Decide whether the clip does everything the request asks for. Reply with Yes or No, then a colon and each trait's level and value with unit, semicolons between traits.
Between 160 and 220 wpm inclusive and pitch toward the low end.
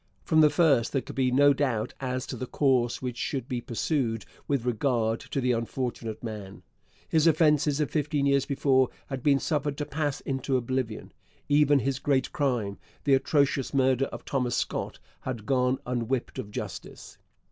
Yes: average, 170 wpm; low, 130 Hz